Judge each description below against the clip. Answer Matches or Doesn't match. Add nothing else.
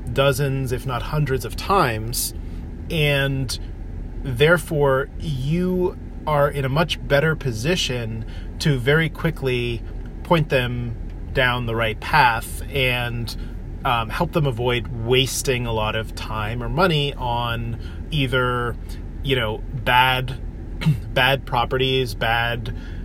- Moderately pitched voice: Doesn't match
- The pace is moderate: Doesn't match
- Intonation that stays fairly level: Doesn't match